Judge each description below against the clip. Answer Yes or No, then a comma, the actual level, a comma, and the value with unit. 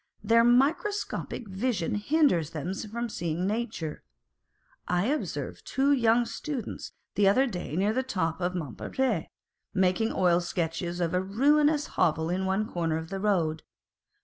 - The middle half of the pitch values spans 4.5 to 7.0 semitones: Yes, wide, 5.6 semitones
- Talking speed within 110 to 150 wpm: Yes, average, 145 wpm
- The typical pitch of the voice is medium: No, high, 195 Hz